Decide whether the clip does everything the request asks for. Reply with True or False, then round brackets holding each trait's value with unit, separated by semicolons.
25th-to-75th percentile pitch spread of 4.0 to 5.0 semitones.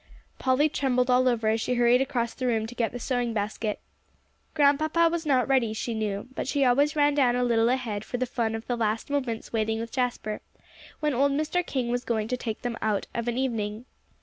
False (3.0 semitones)